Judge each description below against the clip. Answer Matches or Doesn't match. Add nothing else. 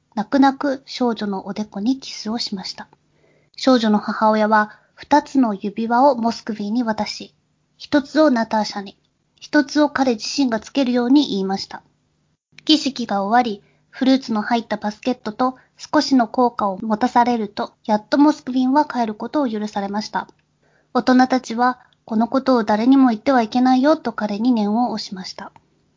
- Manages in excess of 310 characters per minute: Matches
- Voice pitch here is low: Doesn't match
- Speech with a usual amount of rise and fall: Matches